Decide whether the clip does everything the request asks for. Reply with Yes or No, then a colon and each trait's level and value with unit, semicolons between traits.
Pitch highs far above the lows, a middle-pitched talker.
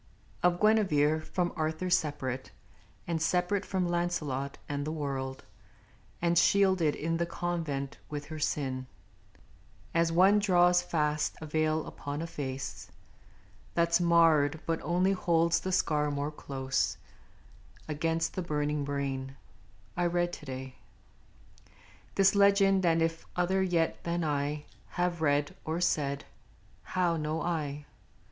No: average, 3.2 semitones; medium, 165 Hz